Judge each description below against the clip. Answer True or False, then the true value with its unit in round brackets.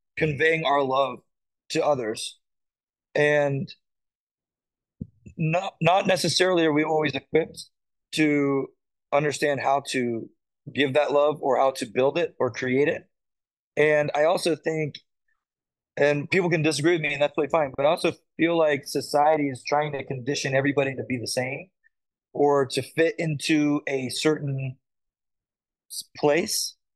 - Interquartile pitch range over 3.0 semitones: False (2.7 semitones)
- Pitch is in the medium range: True (145 Hz)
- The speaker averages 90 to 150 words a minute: True (140 wpm)